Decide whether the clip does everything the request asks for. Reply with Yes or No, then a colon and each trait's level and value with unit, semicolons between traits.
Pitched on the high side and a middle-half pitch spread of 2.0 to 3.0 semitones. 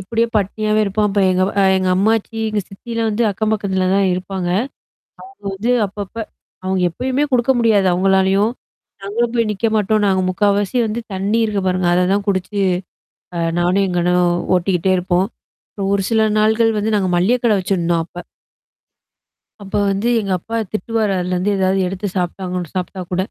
Yes: high, 195 Hz; narrow, 2.6 semitones